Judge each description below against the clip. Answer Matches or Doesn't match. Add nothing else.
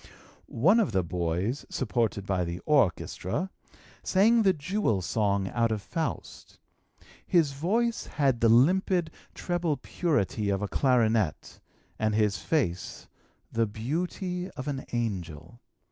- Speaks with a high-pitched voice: Doesn't match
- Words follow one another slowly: Matches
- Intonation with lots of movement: Matches